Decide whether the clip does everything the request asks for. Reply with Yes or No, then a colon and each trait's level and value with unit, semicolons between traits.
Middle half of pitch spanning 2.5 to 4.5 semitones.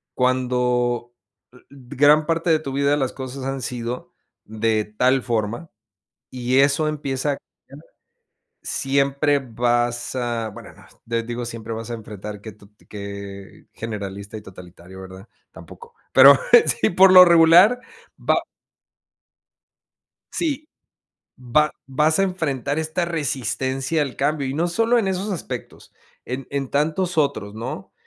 No: average, 4.9 semitones